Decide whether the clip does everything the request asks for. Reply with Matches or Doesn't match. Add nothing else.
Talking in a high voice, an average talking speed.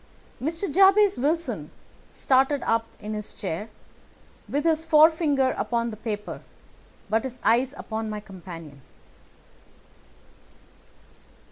Doesn't match